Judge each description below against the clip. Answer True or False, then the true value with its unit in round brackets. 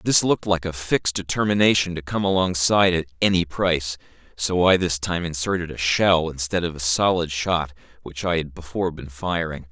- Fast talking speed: False (185 wpm)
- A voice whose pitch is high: False (85 Hz)